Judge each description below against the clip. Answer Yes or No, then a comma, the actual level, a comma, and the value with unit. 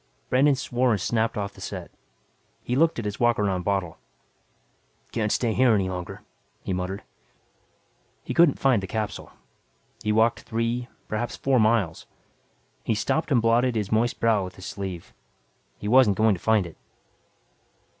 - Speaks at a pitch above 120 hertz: No, low, 110 Hz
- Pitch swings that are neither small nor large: Yes, average, 3.4 semitones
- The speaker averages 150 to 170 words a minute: Yes, average, 160 wpm